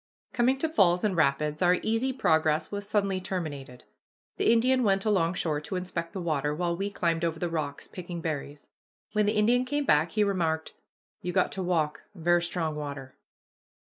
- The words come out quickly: No, average, 175 wpm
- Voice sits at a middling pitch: Yes, medium, 175 Hz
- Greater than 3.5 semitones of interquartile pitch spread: Yes, average, 4.4 semitones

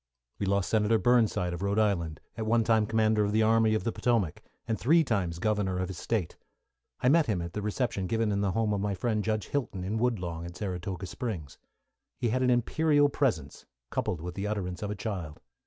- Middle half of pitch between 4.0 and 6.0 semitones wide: No, average, 3.6 semitones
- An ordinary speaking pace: No, fast, 215 wpm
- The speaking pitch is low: Yes, low, 105 Hz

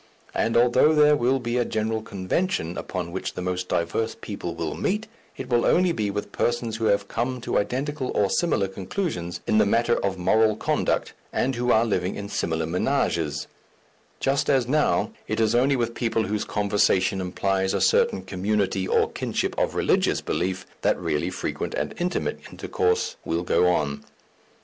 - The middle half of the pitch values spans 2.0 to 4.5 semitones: No, average, 4.9 semitones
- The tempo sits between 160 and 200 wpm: Yes, average, 175 wpm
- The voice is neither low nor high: No, low, 105 Hz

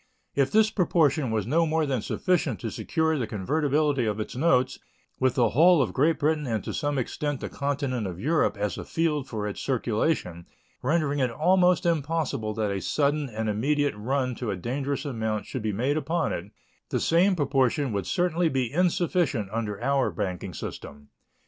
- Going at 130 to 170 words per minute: No, average, 180 wpm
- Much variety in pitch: Yes, wide, 5.9 semitones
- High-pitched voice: No, low, 135 Hz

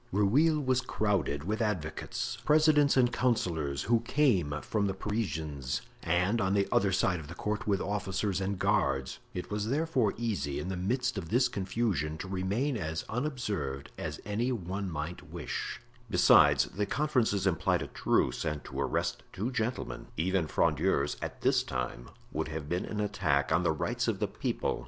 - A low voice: Yes, low, 100 Hz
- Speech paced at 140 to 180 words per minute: Yes, average, 170 wpm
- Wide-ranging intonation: Yes, wide, 6.2 semitones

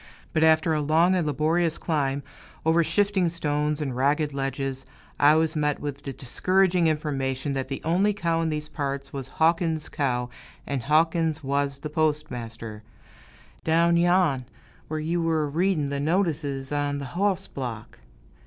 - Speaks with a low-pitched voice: No, medium, 150 Hz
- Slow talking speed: No, average, 155 wpm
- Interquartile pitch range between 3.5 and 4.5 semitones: No, average, 3.0 semitones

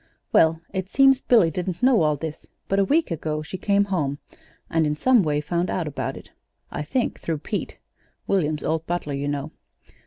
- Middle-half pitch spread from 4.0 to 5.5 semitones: Yes, average, 4.5 semitones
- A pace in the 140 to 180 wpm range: No, average, 190 wpm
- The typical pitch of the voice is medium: Yes, medium, 165 Hz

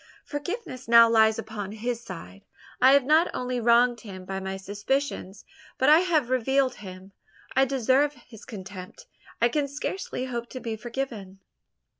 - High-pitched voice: Yes, high, 235 Hz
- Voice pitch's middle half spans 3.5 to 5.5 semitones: Yes, average, 4.7 semitones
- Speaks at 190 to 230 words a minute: No, average, 155 wpm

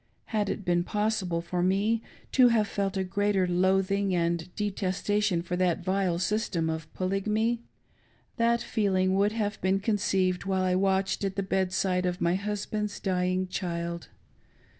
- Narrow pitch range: Yes, narrow, 2.2 semitones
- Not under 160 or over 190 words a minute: No, average, 150 wpm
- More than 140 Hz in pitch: Yes, high, 190 Hz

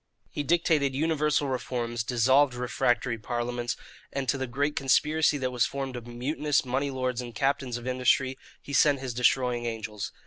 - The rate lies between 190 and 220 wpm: No, average, 165 wpm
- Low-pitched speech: Yes, low, 130 Hz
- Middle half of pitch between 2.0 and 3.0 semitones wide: Yes, narrow, 2.6 semitones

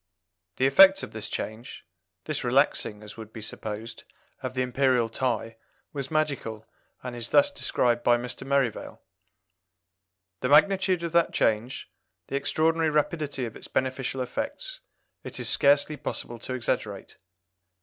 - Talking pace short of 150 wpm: Yes, average, 140 wpm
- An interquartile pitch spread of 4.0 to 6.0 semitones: Yes, average, 4.6 semitones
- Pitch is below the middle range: Yes, low, 130 Hz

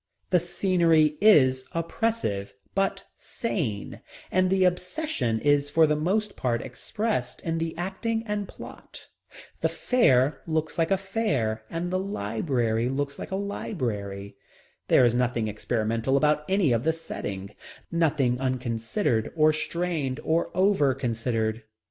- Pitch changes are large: Yes, wide, 7.3 semitones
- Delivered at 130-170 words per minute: Yes, slow, 135 wpm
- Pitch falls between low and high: Yes, medium, 150 Hz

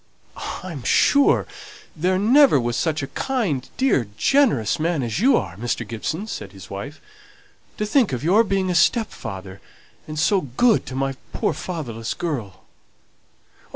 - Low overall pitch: No, medium, 155 Hz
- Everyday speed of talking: Yes, average, 150 wpm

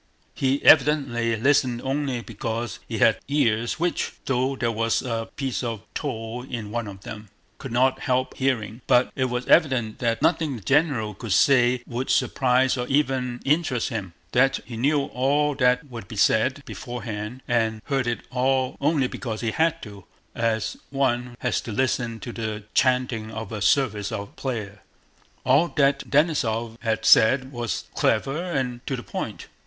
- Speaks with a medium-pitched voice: No, low, 125 Hz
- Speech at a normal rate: Yes, average, 165 wpm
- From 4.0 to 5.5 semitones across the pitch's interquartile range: No, average, 3.0 semitones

